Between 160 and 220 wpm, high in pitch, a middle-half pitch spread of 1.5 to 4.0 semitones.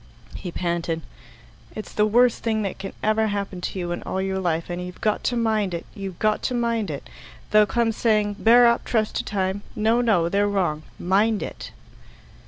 Yes: average, 195 wpm; high, 205 Hz; average, 3.3 semitones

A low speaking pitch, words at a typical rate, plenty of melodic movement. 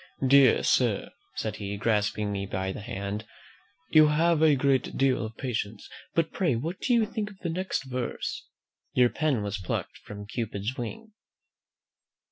Yes: low, 125 Hz; average, 160 wpm; wide, 7.1 semitones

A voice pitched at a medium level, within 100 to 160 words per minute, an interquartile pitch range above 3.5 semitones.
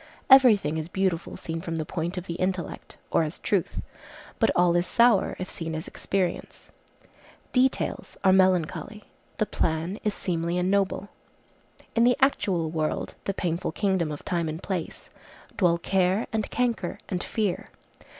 No: medium, 180 Hz; average, 150 wpm; average, 3.2 semitones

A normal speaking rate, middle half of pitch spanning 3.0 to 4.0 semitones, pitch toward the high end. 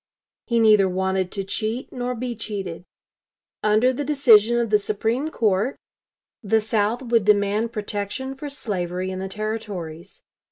Yes: average, 145 wpm; average, 3.4 semitones; high, 215 Hz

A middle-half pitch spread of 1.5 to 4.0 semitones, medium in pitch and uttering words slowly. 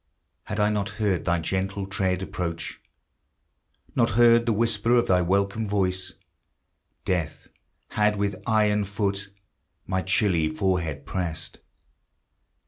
No: narrow, 2.5 semitones; low, 100 Hz; slow, 120 wpm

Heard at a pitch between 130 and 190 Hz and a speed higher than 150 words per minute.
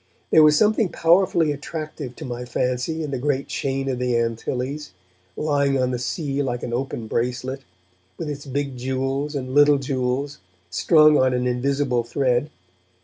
Yes: low, 135 Hz; average, 160 wpm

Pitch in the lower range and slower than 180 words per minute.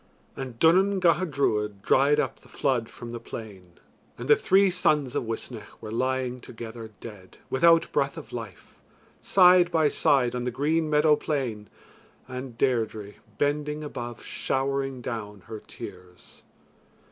Yes: low, 130 Hz; average, 145 wpm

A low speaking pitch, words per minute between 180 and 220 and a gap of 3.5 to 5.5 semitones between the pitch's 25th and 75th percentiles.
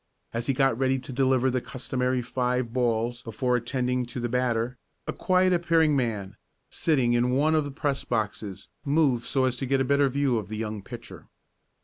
No: low, 125 Hz; average, 195 wpm; narrow, 2.4 semitones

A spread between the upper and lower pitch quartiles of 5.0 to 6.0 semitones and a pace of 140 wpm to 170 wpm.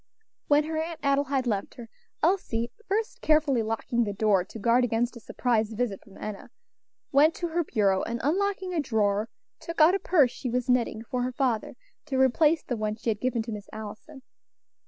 No: wide, 5.5 semitones; average, 195 wpm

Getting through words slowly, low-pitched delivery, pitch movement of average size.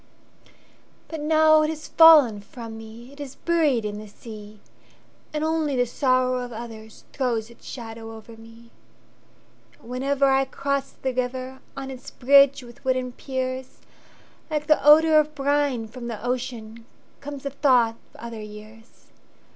No: slow, 130 wpm; very high, 255 Hz; average, 3.7 semitones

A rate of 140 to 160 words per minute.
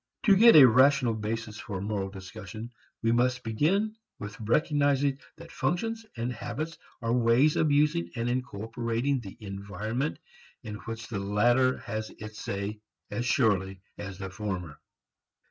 Yes: average, 145 wpm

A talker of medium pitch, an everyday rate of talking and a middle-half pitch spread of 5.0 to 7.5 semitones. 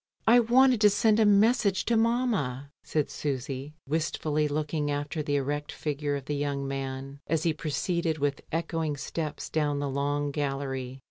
No: medium, 150 Hz; average, 160 wpm; average, 3.2 semitones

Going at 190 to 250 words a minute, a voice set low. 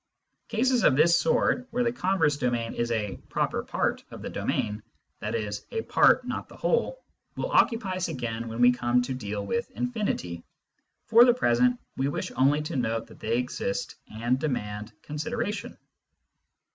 No: average, 170 wpm; low, 130 Hz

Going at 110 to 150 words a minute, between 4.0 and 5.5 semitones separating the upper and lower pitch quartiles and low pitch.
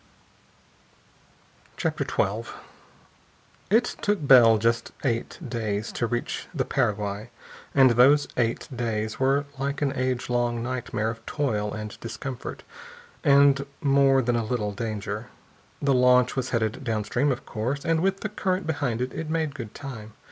No: average, 145 wpm; average, 3.6 semitones; low, 125 Hz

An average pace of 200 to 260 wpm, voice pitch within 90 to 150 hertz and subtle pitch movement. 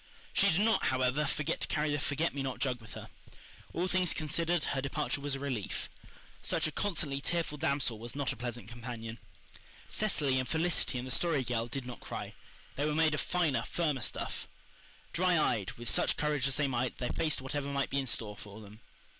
No: fast, 205 wpm; medium, 140 Hz; average, 3.8 semitones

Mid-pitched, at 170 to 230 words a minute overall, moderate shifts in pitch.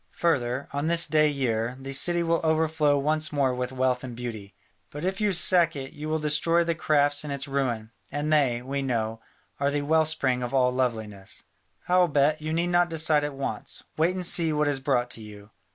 Yes: medium, 145 Hz; fast, 205 wpm; average, 3.9 semitones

